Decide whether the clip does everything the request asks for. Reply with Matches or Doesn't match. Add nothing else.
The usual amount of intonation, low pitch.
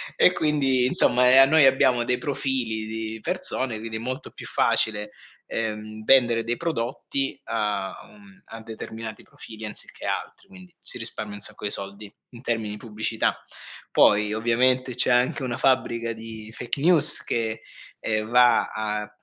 Matches